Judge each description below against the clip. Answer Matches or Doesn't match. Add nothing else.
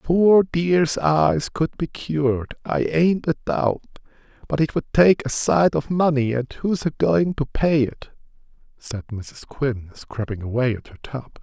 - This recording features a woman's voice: Doesn't match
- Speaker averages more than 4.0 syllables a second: Doesn't match